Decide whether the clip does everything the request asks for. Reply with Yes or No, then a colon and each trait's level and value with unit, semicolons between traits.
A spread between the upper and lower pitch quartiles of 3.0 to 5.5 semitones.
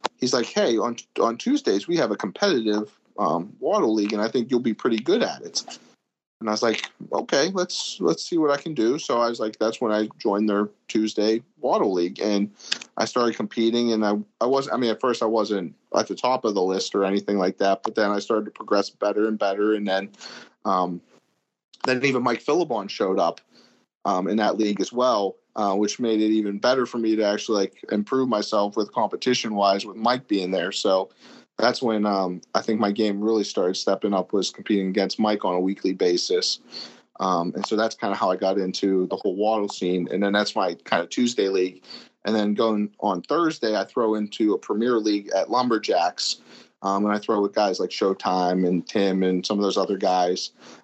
No: narrow, 2.4 semitones